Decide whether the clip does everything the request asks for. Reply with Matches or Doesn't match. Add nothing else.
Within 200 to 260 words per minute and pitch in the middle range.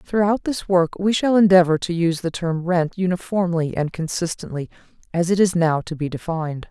Doesn't match